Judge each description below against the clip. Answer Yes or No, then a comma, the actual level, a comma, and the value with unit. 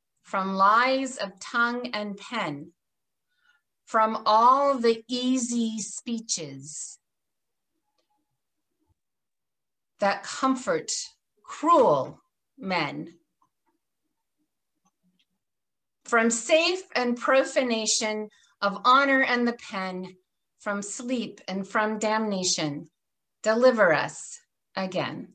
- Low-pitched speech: No, high, 225 Hz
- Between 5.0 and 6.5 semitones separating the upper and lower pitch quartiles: Yes, average, 5.3 semitones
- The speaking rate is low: Yes, slow, 75 wpm